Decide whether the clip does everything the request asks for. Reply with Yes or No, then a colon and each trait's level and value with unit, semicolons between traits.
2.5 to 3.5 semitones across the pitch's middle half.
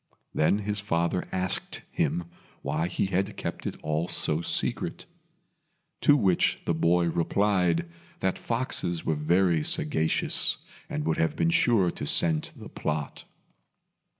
Yes: average, 3.0 semitones